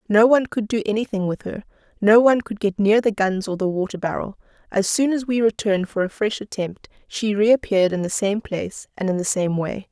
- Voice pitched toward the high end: Yes, high, 205 Hz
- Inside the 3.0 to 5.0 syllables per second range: No, 5.7 syllables/s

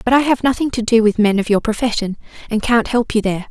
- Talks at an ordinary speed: No, fast, 275 wpm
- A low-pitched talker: No, high, 225 Hz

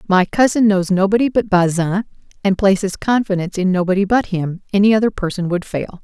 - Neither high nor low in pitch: No, high, 195 Hz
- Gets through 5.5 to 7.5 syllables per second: Yes, 5.7 syllables/s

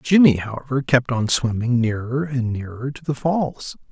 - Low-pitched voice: Yes, low, 130 Hz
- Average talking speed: Yes, average, 170 wpm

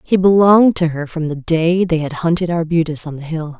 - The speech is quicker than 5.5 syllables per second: No, 5.4 syllables/s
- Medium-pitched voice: Yes, medium, 165 Hz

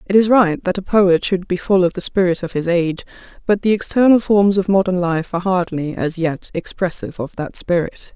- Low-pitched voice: No, medium, 185 Hz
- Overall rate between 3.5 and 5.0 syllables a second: No, 5.4 syllables/s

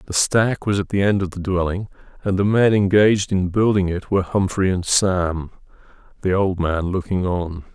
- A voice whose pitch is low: Yes, very low, 95 Hz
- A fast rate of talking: No, average, 195 wpm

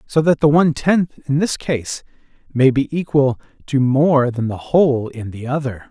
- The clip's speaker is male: Yes, male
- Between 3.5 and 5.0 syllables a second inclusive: Yes, 4.6 syllables/s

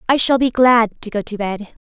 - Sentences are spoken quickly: Yes, fast, 265 wpm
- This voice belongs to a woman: Yes, female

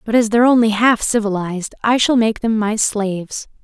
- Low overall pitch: No, high, 220 Hz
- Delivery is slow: No, average, 200 wpm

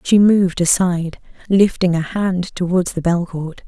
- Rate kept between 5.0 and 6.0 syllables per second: No, 4.6 syllables/s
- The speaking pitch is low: No, medium, 180 Hz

